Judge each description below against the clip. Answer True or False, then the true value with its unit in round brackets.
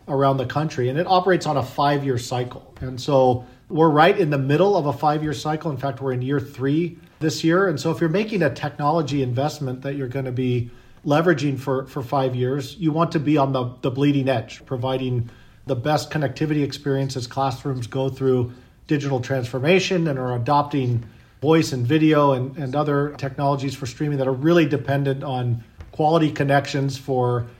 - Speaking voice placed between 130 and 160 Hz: True (140 Hz)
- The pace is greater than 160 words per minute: True (190 wpm)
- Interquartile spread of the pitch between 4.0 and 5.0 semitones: False (2.6 semitones)